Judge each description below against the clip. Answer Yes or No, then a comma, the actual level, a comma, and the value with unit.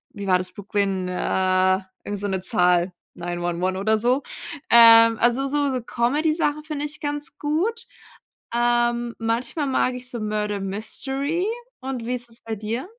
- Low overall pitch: No, high, 235 Hz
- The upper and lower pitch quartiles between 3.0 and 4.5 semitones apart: No, wide, 5.5 semitones